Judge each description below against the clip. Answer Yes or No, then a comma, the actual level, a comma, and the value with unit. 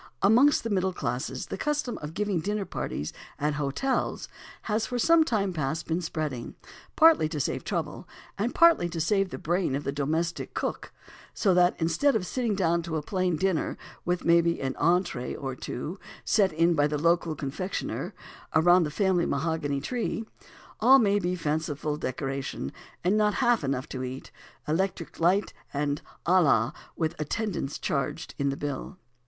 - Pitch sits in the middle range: Yes, medium, 170 Hz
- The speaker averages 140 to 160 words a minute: No, average, 170 wpm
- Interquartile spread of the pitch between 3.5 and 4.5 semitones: No, average, 5.1 semitones